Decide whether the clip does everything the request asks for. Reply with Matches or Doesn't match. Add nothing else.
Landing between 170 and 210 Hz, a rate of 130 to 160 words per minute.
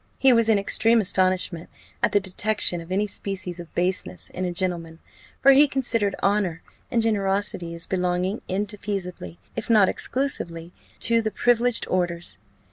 Matches